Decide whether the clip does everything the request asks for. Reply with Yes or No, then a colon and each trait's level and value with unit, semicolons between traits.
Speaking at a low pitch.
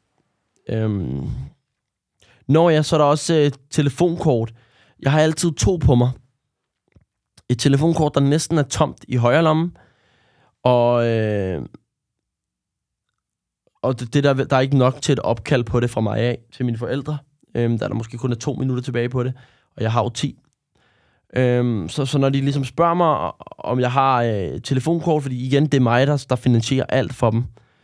Yes: low, 130 Hz